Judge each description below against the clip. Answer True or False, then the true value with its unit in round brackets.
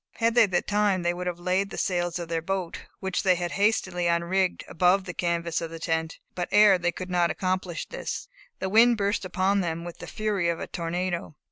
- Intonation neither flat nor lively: False (2.2 semitones)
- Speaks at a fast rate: True (215 wpm)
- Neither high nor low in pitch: True (180 Hz)